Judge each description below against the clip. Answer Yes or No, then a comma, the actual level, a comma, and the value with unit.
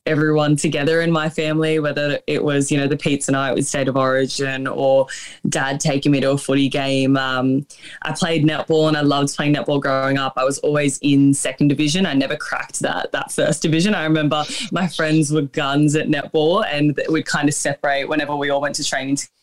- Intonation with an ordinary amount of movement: No, narrow, 2.1 semitones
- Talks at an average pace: No, fast, 215 wpm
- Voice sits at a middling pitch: Yes, medium, 145 Hz